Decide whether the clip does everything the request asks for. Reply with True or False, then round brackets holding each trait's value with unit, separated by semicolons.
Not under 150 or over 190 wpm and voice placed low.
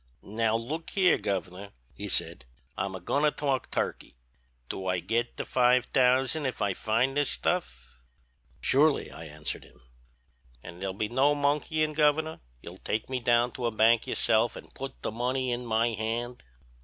True (170 wpm; 120 Hz)